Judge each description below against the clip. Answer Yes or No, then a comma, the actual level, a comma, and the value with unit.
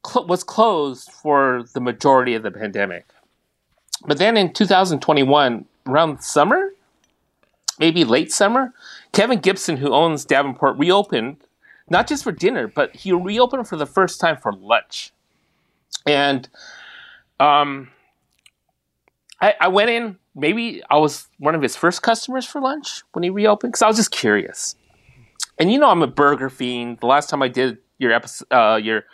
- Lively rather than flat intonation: Yes, wide, 8.1 semitones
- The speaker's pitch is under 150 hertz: No, medium, 165 Hz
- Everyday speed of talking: Yes, average, 155 wpm